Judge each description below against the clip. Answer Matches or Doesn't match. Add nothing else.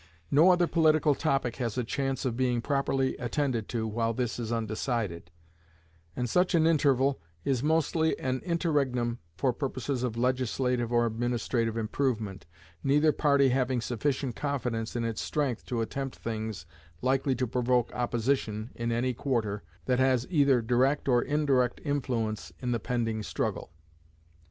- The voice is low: Matches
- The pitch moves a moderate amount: Matches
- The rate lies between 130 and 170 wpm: Matches